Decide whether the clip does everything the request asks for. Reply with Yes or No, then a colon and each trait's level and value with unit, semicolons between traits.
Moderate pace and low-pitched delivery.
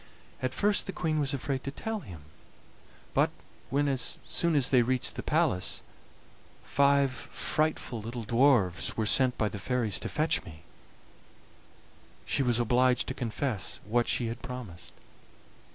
Yes: average, 150 wpm; low, 125 Hz